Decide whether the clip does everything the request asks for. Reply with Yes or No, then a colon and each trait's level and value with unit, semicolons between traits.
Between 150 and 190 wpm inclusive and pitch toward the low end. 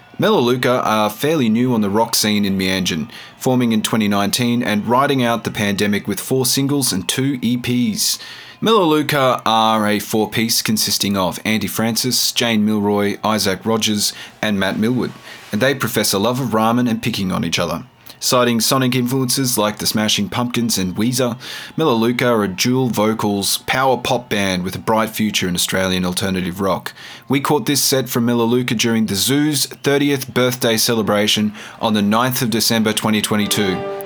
Yes: average, 165 wpm; low, 115 Hz